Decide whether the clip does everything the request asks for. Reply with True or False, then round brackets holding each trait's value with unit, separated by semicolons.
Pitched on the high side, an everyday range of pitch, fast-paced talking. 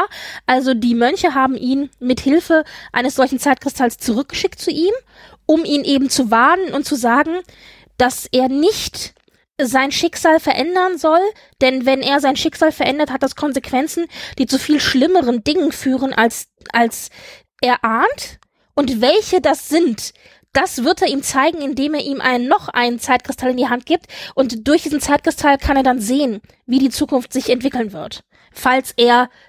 False (275 Hz; 3.5 semitones; 170 wpm)